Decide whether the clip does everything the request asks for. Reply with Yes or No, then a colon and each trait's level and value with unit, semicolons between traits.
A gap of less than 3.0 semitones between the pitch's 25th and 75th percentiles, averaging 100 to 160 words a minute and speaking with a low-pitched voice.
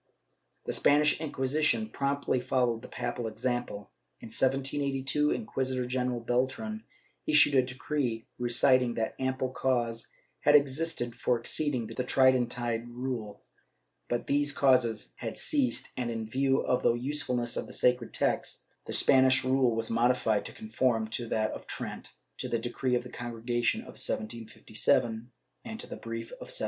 Yes: narrow, 2.5 semitones; average, 155 wpm; low, 125 Hz